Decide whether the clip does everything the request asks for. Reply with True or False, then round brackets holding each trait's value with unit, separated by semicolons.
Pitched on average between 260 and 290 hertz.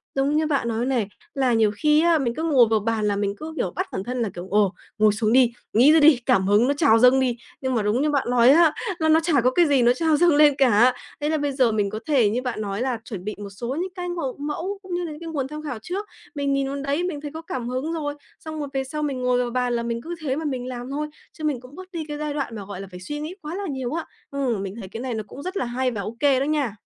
True (265 Hz)